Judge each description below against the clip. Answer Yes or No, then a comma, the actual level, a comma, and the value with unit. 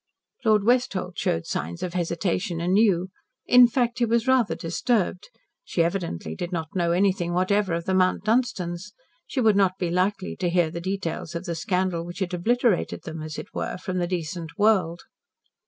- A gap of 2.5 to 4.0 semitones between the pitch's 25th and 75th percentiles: Yes, average, 3.4 semitones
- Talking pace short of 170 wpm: No, average, 180 wpm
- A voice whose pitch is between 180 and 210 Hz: Yes, medium, 185 Hz